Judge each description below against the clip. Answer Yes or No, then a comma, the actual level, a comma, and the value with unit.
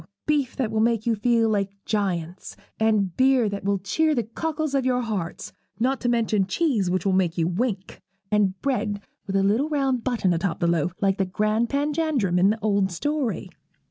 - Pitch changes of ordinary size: Yes, average, 4.8 semitones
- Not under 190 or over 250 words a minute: Yes, average, 200 wpm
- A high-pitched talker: Yes, high, 215 Hz